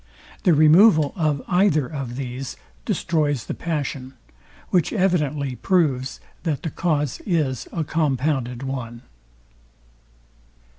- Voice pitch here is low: No, medium, 145 Hz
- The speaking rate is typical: No, slow, 105 wpm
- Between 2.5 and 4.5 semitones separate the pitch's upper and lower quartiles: Yes, average, 3.8 semitones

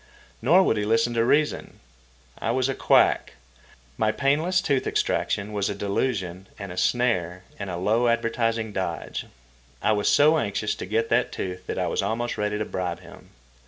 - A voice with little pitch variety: No, average, 3.7 semitones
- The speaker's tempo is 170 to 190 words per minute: Yes, average, 180 wpm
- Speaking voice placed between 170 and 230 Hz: No, low, 110 Hz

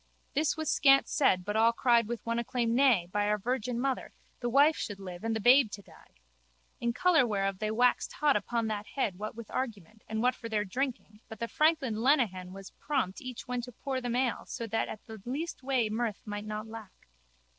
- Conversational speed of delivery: No, fast, 215 wpm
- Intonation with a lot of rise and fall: No, average, 3.5 semitones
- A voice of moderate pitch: No, high, 230 Hz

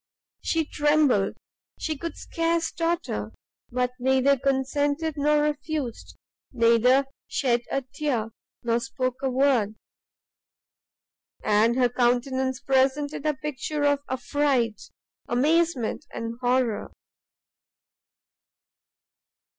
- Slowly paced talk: Yes, slow, 90 wpm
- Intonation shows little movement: No, average, 3.4 semitones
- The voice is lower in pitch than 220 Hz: No, very high, 265 Hz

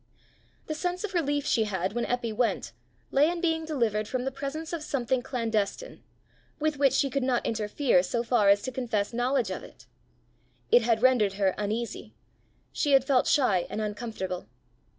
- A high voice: Yes, high, 245 Hz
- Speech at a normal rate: Yes, average, 175 wpm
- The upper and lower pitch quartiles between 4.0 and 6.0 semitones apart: Yes, average, 4.6 semitones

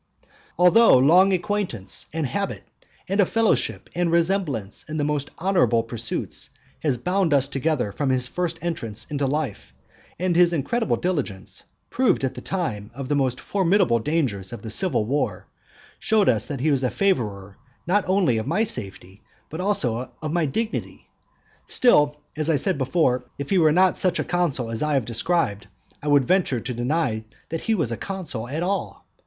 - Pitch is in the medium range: Yes, medium, 150 Hz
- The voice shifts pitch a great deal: Yes, wide, 6.5 semitones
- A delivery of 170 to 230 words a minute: Yes, average, 175 wpm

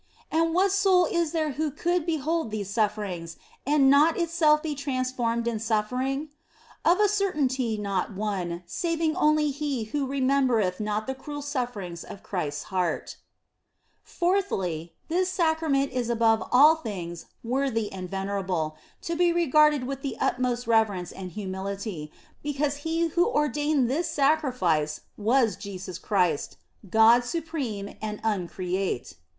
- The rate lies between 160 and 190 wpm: No, average, 140 wpm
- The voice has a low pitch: No, very high, 255 Hz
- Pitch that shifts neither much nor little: No, wide, 7.2 semitones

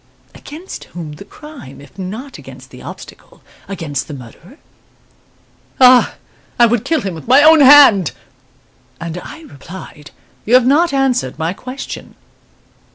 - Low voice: No, high, 230 Hz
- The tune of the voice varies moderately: No, wide, 9.0 semitones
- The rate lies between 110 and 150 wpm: Yes, average, 140 wpm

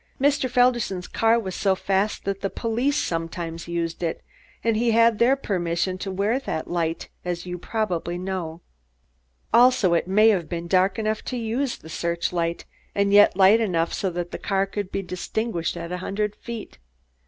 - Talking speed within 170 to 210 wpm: Yes, average, 180 wpm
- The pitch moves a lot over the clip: No, average, 4.5 semitones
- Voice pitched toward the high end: Yes, high, 195 Hz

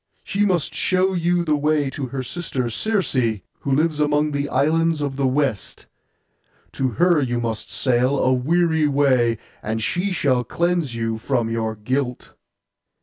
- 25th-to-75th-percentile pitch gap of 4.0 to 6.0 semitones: Yes, average, 5.0 semitones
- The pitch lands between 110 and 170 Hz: Yes, medium, 140 Hz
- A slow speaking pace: No, average, 155 wpm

